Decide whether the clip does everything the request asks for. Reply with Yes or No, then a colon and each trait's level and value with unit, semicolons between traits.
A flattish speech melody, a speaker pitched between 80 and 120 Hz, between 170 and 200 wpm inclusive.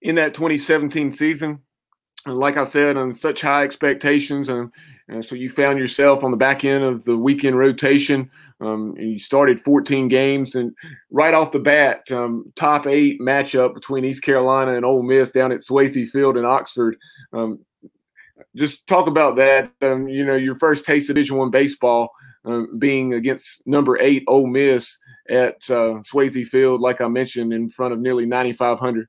No: narrow, 2.1 semitones; low, 135 Hz; average, 175 wpm